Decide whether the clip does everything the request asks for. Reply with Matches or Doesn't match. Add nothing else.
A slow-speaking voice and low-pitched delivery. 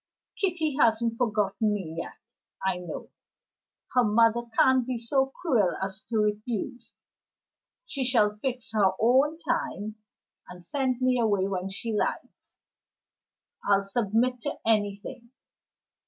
Doesn't match